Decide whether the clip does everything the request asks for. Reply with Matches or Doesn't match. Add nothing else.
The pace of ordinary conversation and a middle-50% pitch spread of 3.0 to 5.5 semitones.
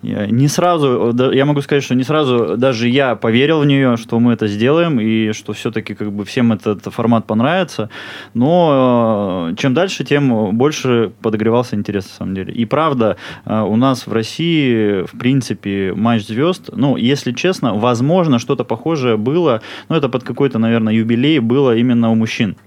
Doesn't match